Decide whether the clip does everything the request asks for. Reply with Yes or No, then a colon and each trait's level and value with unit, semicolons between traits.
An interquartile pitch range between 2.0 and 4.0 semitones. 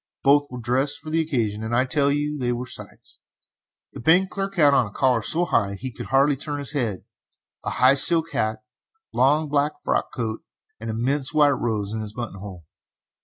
No: average, 4.6 semitones